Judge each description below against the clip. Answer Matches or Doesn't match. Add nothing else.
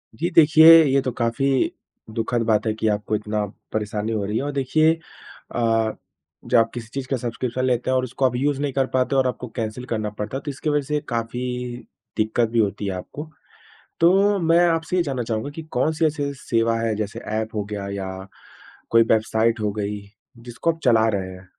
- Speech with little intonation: Doesn't match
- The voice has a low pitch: Matches